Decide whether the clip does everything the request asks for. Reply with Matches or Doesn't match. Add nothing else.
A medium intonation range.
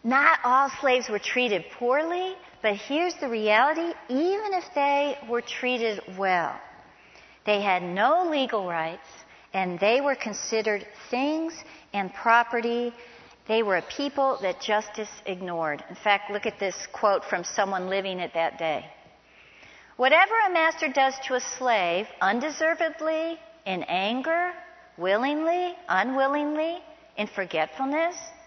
Doesn't match